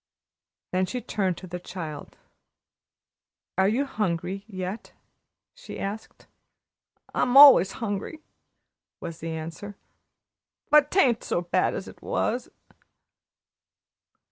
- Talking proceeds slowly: Yes, slow, 105 wpm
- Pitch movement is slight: No, wide, 5.6 semitones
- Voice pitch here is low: No, high, 195 Hz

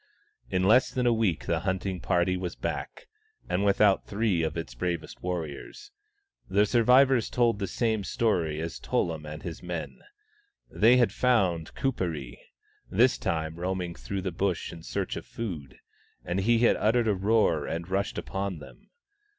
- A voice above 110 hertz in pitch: No, very low, 95 Hz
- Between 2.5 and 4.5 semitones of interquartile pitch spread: No, average, 5.0 semitones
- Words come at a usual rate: Yes, average, 160 wpm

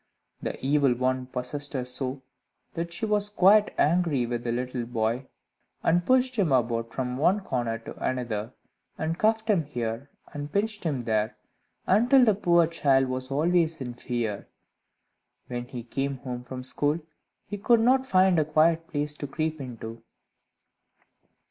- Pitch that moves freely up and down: Yes, wide, 5.8 semitones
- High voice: No, medium, 140 Hz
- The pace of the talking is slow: No, average, 155 wpm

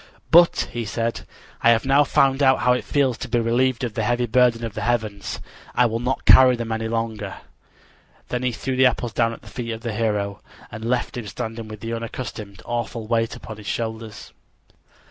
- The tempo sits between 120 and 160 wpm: No, fast, 205 wpm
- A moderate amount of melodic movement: No, narrow, 1.9 semitones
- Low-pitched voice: Yes, low, 115 Hz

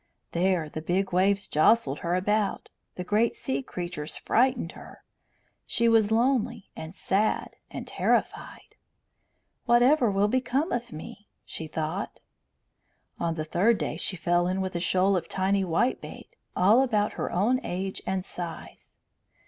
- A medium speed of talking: Yes, average, 145 wpm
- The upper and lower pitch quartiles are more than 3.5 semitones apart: Yes, average, 4.6 semitones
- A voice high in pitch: Yes, high, 195 Hz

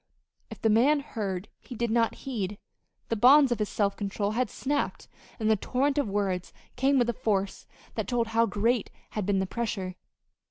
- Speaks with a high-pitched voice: Yes, high, 225 Hz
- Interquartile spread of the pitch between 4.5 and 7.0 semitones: No, average, 3.5 semitones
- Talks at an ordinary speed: Yes, average, 190 wpm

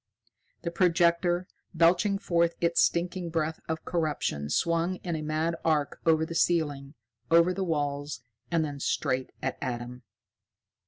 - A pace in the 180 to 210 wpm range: No, average, 140 wpm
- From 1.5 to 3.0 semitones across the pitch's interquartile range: Yes, average, 2.7 semitones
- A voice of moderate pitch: Yes, medium, 165 Hz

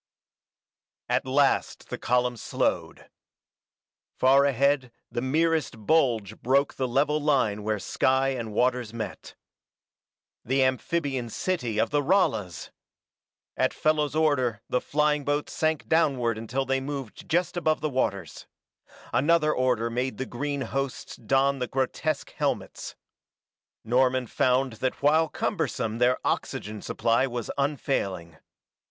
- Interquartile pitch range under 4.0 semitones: Yes, average, 3.4 semitones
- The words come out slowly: Yes, slow, 125 wpm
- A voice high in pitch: No, low, 130 Hz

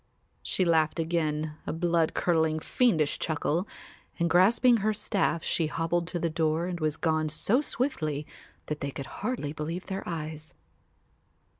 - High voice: No, medium, 165 Hz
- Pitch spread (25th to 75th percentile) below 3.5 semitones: Yes, average, 2.7 semitones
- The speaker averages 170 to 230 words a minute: No, average, 150 wpm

